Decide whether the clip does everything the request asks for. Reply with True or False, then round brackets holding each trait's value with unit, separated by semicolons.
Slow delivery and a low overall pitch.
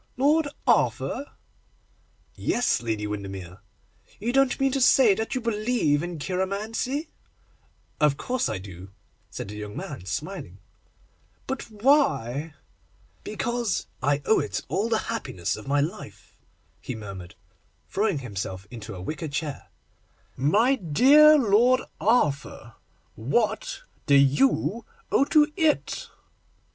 False (125 wpm; 190 Hz)